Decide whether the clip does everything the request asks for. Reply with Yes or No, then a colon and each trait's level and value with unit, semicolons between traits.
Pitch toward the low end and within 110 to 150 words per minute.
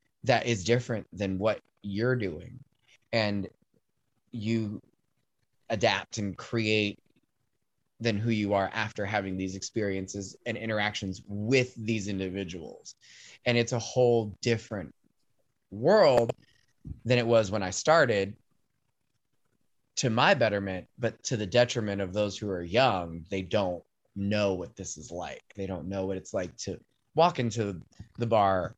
Yes: low, 105 Hz; average, 140 wpm